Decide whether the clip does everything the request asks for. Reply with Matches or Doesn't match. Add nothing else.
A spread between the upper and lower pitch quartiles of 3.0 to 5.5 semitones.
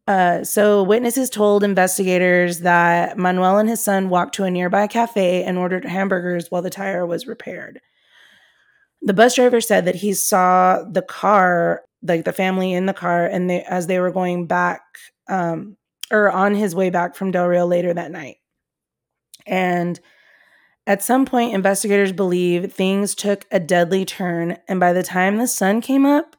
Doesn't match